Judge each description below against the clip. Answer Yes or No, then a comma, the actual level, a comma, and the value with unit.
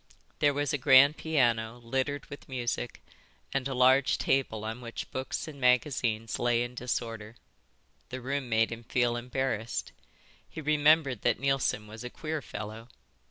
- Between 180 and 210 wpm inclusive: No, average, 155 wpm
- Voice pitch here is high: No, low, 125 Hz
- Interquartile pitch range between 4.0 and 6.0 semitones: No, average, 3.0 semitones